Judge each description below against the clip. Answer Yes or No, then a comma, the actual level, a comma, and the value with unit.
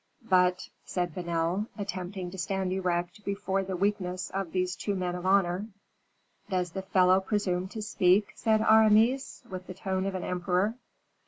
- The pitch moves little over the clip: Yes, narrow, 1.8 semitones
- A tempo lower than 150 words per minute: No, average, 165 wpm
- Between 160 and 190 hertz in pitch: Yes, medium, 185 Hz